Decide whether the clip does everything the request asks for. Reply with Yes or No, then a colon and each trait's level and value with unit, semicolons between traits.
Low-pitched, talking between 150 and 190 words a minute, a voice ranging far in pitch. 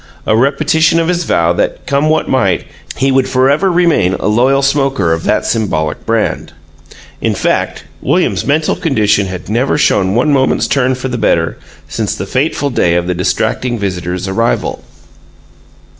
Yes: low, 120 Hz; average, 160 wpm; wide, 6.6 semitones